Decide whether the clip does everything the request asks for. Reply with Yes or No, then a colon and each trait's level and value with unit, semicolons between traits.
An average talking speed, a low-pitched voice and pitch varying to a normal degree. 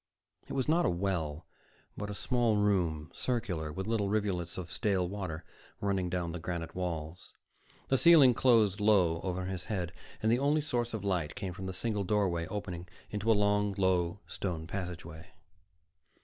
Yes: average, 170 wpm; very low, 95 Hz; average, 3.4 semitones